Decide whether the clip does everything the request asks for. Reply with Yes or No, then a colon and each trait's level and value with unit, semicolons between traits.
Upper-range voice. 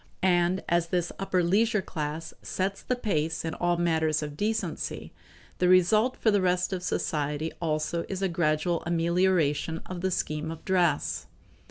No: medium, 175 Hz